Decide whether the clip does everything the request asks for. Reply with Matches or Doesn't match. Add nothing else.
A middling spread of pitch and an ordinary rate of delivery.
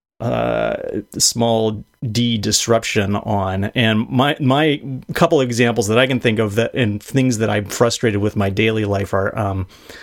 Matches